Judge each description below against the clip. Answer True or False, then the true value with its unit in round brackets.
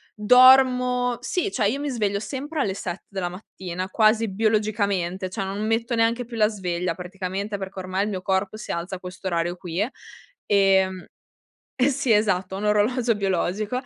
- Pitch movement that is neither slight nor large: True (3.5 semitones)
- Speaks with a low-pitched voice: False (205 Hz)